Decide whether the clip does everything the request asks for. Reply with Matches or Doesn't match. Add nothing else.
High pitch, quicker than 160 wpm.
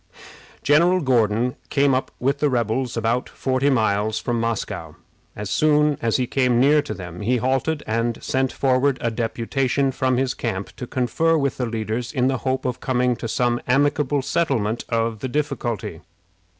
Doesn't match